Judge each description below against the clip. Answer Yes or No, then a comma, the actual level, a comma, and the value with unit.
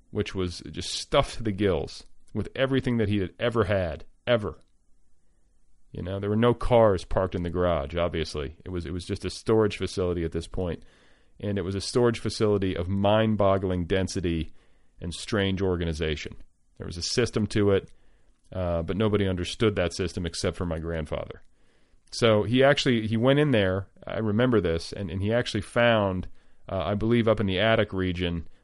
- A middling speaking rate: Yes, average, 190 wpm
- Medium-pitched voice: No, very low, 95 Hz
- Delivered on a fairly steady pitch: No, average, 4.1 semitones